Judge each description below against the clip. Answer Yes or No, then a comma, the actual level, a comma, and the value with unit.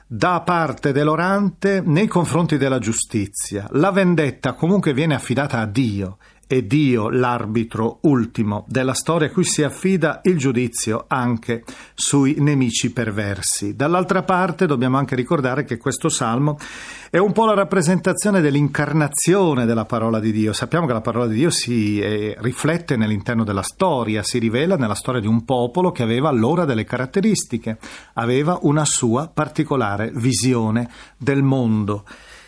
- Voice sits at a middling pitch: No, low, 130 Hz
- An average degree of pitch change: No, wide, 5.7 semitones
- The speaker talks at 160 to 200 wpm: No, average, 145 wpm